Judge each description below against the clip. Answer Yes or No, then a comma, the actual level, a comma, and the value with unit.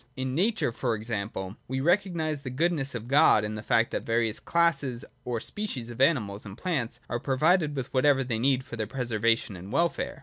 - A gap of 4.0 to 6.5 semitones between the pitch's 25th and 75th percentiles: Yes, average, 4.8 semitones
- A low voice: Yes, low, 130 Hz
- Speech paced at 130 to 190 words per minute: No, average, 200 wpm